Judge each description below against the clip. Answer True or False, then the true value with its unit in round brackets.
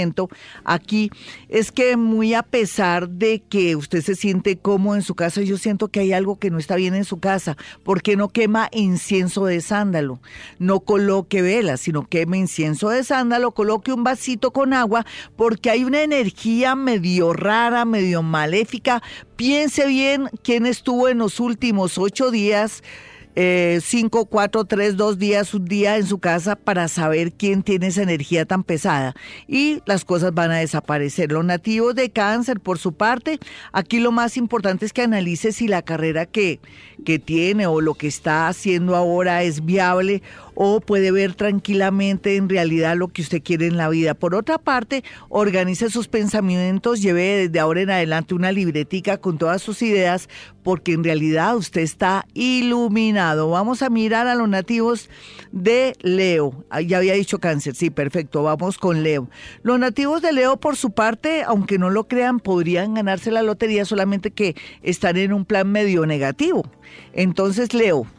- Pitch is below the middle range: False (195 Hz)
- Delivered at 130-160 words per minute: False (170 wpm)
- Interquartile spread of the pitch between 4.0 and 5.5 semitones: True (4.3 semitones)